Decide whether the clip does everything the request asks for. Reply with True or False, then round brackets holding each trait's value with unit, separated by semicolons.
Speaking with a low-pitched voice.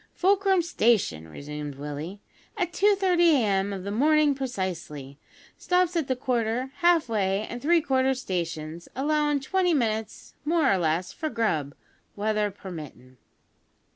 False (230 Hz)